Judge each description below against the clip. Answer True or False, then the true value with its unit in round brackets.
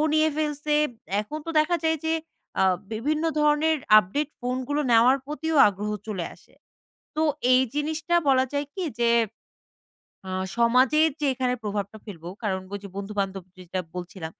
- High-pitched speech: True (255 Hz)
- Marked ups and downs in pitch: True (7.0 semitones)